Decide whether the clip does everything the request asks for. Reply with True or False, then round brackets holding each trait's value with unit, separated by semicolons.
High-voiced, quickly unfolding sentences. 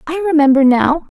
False (300 Hz; 150 wpm)